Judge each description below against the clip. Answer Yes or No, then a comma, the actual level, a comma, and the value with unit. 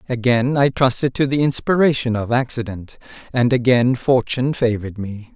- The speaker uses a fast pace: No, average, 145 wpm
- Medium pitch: No, low, 125 Hz